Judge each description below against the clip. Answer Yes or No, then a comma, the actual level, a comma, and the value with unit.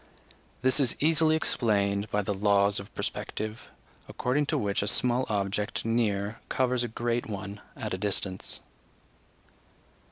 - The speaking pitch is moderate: No, low, 105 Hz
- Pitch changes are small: No, average, 3.4 semitones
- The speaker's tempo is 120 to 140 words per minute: Yes, slow, 135 wpm